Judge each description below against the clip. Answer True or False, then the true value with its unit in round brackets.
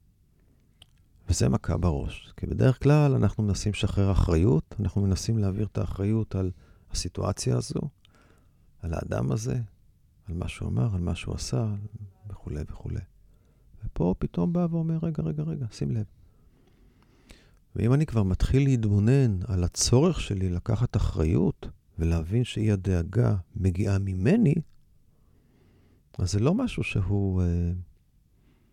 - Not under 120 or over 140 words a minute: True (125 wpm)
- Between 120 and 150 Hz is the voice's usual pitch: False (100 Hz)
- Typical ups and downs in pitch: True (4.3 semitones)